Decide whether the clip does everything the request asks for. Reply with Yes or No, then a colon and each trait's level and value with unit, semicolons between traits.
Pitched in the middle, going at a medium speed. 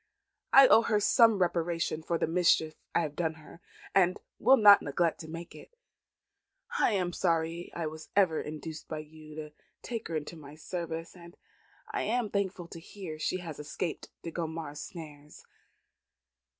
Yes: medium, 165 Hz; average, 165 wpm